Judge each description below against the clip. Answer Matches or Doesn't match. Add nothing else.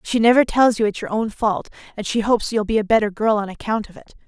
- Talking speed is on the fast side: Matches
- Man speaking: Doesn't match